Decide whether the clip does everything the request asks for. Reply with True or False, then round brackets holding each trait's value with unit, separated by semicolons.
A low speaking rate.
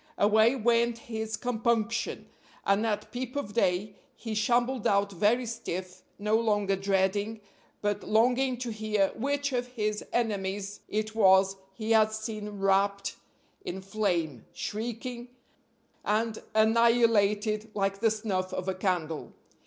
True (130 wpm)